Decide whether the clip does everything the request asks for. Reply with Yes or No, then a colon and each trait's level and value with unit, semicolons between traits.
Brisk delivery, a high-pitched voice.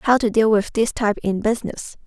Yes: fast, 230 wpm; high, 220 Hz